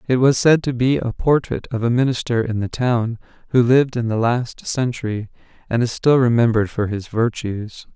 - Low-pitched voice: Yes, low, 120 Hz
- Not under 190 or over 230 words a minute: Yes, average, 195 wpm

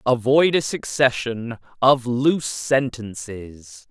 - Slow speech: Yes, slow, 90 wpm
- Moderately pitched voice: No, low, 120 Hz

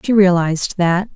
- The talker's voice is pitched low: No, medium, 185 Hz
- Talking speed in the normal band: Yes, average, 155 wpm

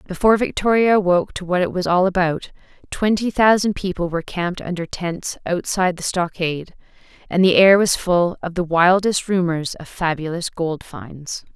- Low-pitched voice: No, medium, 180 Hz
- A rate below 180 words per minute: Yes, average, 165 wpm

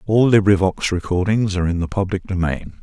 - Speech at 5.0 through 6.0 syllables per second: Yes, 5.6 syllables/s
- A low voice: Yes, very low, 95 Hz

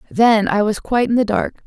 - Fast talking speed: Yes, fast, 250 wpm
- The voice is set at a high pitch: Yes, high, 220 Hz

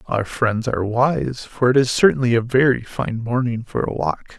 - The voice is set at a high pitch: No, low, 120 Hz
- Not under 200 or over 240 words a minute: Yes, fast, 205 wpm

